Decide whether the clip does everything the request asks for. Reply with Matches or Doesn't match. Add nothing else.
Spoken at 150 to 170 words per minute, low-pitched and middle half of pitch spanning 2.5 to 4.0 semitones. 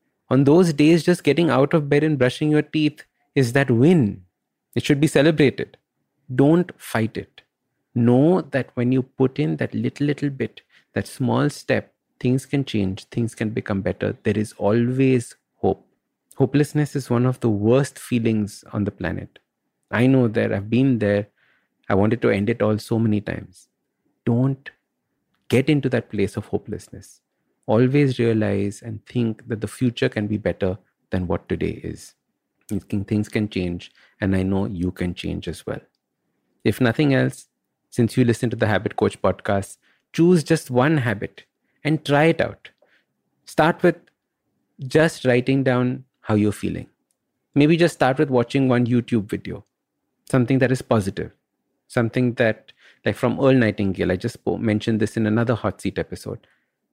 Doesn't match